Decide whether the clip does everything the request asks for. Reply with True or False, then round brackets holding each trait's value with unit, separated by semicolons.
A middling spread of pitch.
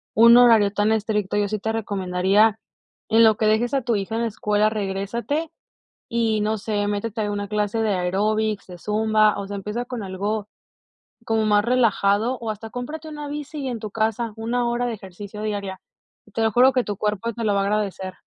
False (2.1 semitones)